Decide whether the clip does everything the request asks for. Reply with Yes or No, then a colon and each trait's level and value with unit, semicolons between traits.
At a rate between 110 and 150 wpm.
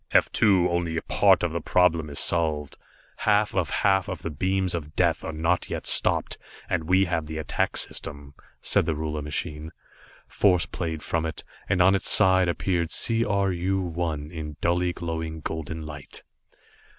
No: average, 175 wpm